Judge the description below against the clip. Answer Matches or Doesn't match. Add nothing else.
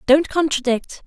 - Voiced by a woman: Matches